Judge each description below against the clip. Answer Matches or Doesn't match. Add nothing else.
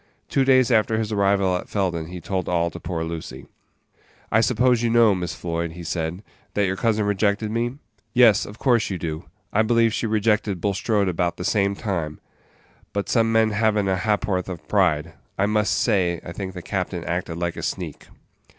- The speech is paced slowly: Doesn't match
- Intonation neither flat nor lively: Matches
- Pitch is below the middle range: Matches